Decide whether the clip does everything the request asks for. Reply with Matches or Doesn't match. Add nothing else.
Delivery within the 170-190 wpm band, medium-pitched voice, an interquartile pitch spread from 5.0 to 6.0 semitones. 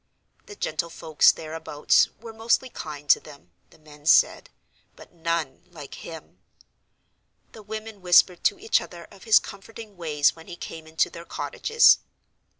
Doesn't match